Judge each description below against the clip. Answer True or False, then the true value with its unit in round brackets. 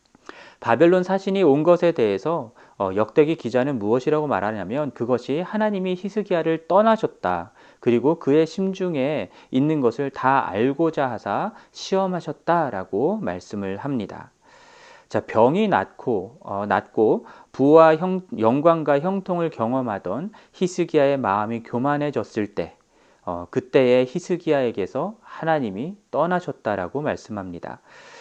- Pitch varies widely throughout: True (6.6 semitones)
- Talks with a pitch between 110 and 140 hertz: False (155 Hz)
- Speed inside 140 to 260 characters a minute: False (285 characters per minute)